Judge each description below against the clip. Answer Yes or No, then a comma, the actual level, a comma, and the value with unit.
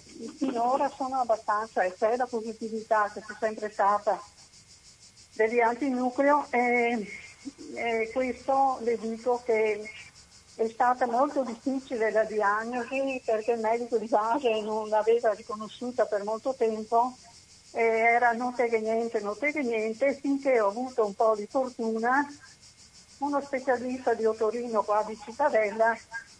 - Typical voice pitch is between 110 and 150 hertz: No, high, 230 Hz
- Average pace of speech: Yes, average, 130 wpm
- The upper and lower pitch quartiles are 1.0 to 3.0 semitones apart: Yes, average, 2.7 semitones